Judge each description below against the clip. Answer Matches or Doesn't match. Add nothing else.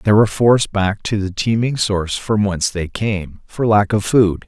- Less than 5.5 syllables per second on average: Matches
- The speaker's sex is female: Doesn't match